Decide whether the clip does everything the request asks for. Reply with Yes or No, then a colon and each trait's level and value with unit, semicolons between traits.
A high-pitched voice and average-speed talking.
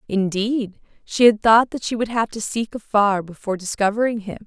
Yes: high, 215 Hz; average, 190 wpm